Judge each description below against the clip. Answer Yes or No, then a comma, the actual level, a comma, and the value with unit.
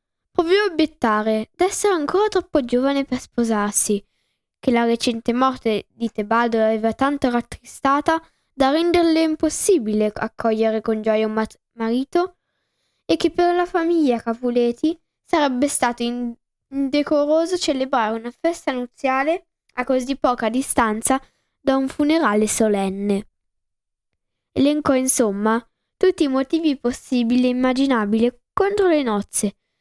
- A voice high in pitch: Yes, very high, 260 Hz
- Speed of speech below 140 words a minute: Yes, average, 120 wpm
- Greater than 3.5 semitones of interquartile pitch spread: Yes, wide, 5.6 semitones